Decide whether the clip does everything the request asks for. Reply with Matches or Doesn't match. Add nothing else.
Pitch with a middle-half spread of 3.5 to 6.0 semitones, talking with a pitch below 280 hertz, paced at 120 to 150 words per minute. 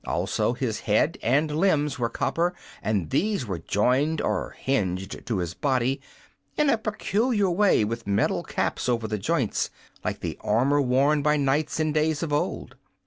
Doesn't match